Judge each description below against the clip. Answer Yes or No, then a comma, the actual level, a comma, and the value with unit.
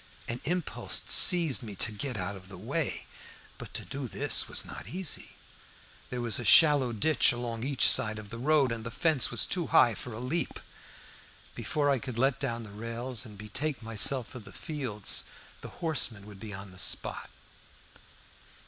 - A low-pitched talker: Yes, low, 120 Hz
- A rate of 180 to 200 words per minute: Yes, average, 185 wpm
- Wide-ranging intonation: No, average, 4.7 semitones